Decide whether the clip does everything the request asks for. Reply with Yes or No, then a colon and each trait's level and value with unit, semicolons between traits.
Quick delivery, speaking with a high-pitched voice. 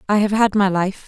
Yes: fast, 280 wpm; high, 200 Hz